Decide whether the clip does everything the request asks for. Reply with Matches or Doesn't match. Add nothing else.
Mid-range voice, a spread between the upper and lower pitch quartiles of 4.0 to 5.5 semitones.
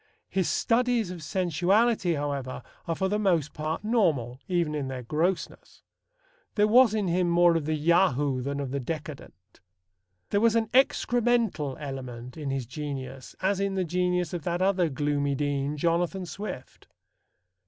Matches